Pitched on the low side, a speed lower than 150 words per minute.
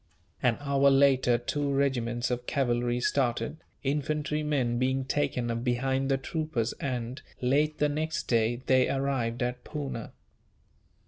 Yes: low, 130 Hz; slow, 135 wpm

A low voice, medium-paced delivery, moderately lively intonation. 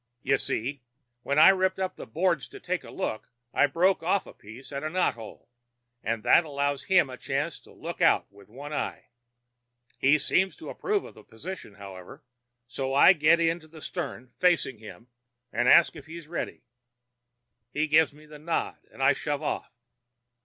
No: medium, 145 Hz; average, 190 wpm; average, 4.8 semitones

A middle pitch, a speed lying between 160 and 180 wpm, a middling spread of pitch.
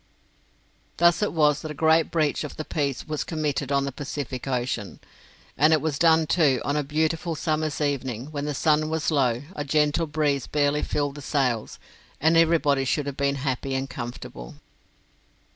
No: medium, 145 Hz; average, 175 wpm; narrow, 2.3 semitones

